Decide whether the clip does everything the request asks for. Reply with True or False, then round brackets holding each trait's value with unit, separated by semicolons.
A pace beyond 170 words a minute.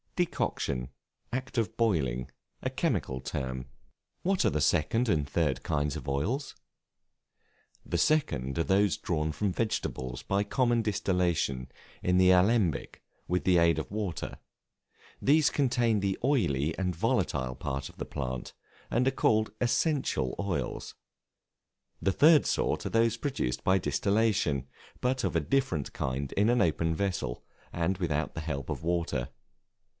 False (145 wpm)